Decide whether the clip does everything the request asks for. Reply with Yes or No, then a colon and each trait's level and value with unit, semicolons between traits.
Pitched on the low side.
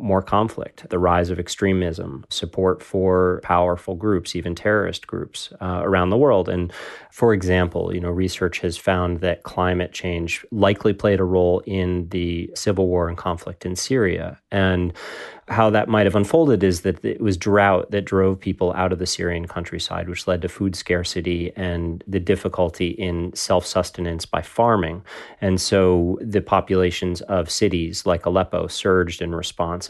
Yes: very low, 90 Hz